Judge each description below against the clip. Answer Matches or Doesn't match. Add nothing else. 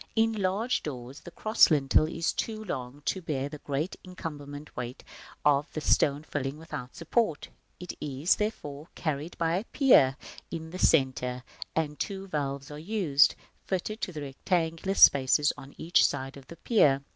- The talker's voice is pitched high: Doesn't match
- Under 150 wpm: Doesn't match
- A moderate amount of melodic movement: Matches